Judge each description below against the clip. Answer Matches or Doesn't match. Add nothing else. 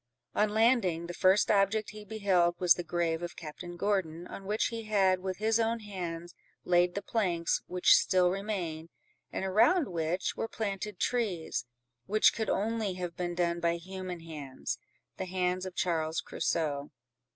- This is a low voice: Doesn't match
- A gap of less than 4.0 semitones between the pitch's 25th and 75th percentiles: Matches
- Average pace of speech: Matches